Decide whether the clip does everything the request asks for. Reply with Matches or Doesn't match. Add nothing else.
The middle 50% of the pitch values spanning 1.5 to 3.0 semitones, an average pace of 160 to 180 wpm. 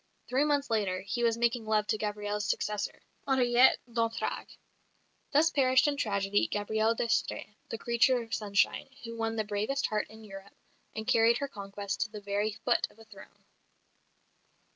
Matches